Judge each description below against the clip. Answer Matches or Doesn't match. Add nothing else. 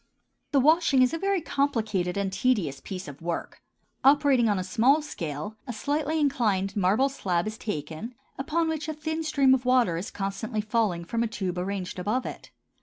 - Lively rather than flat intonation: Matches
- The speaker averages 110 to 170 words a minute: Doesn't match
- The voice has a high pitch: Matches